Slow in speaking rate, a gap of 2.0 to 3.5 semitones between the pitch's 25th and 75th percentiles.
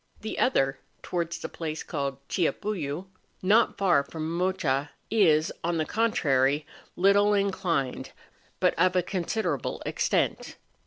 No: slow, 120 wpm; average, 5.2 semitones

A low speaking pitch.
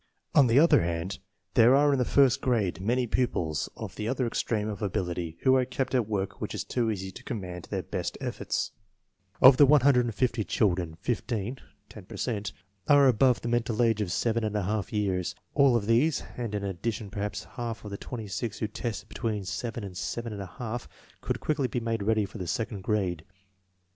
Yes: low, 110 Hz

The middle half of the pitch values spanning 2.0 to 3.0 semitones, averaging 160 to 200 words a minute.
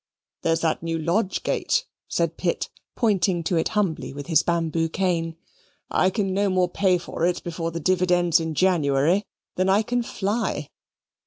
Yes: narrow, 2.6 semitones; average, 170 wpm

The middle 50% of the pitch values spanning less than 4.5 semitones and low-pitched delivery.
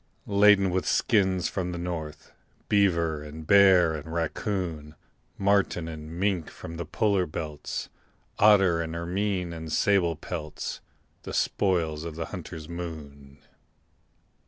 Yes: average, 3.3 semitones; very low, 85 Hz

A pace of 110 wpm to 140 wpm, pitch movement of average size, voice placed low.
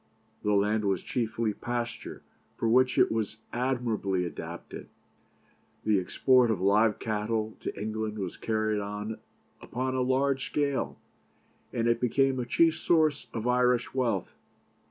Yes: slow, 135 wpm; average, 3.2 semitones; low, 115 Hz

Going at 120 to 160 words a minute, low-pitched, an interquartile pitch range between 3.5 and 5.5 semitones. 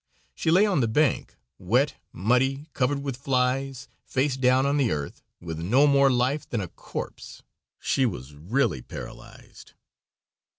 Yes: average, 145 wpm; low, 130 Hz; average, 3.8 semitones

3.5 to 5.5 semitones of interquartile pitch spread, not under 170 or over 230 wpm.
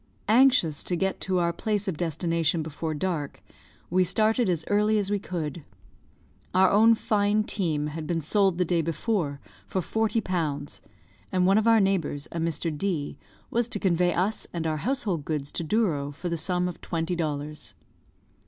Yes: average, 4.3 semitones; average, 175 wpm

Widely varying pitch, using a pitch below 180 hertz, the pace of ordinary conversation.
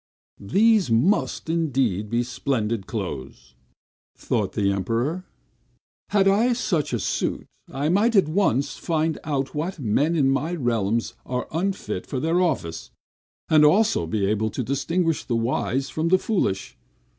Yes: wide, 7.2 semitones; medium, 140 Hz; average, 145 wpm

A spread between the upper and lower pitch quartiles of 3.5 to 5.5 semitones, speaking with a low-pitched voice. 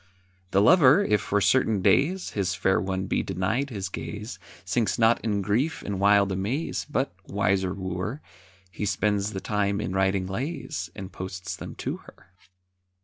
No: average, 2.9 semitones; low, 100 Hz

